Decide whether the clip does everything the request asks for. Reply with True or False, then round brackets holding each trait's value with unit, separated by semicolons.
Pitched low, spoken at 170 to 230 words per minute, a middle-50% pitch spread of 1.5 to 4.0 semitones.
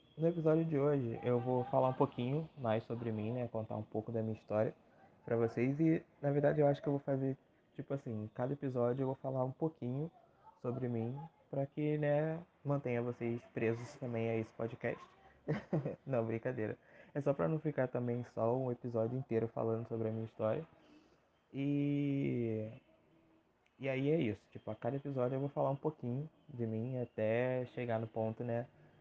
True (125 Hz; 185 wpm; 3.7 semitones)